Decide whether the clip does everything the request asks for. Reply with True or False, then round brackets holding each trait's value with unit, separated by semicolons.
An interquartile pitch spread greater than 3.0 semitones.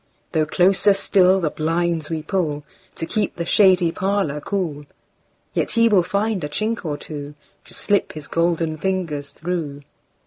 True (4.1 semitones)